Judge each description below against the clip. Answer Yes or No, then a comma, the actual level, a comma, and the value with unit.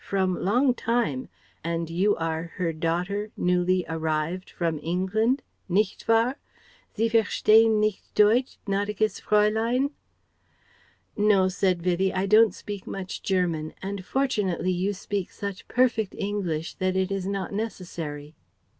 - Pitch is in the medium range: No, high, 195 Hz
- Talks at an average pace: No, slow, 130 wpm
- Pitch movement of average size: Yes, average, 3.2 semitones